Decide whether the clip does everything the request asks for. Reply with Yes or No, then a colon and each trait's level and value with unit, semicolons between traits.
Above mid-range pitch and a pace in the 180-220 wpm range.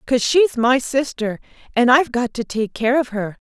Yes: high, 245 Hz; fast, 205 wpm